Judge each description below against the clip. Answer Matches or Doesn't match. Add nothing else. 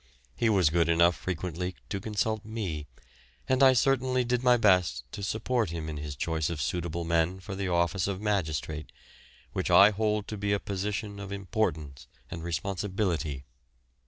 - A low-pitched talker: Matches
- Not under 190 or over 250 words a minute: Doesn't match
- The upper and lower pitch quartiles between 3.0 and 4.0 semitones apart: Doesn't match